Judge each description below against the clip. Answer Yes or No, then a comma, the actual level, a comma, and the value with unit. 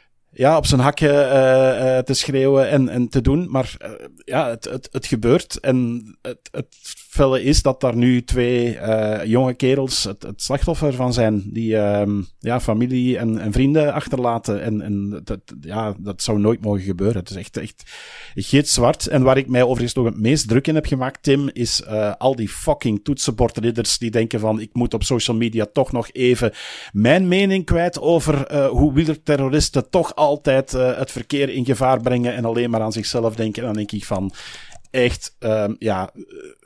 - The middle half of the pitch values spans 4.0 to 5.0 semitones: No, average, 3.6 semitones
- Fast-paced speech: No, average, 190 wpm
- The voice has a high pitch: No, low, 125 Hz